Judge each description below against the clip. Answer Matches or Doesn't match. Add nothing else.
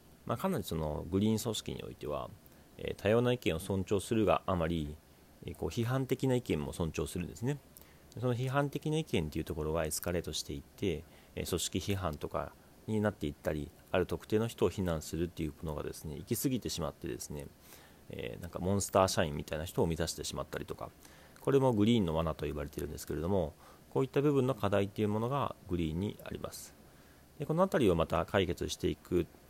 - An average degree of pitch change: Doesn't match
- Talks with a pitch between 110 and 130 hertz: Doesn't match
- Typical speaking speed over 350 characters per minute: Matches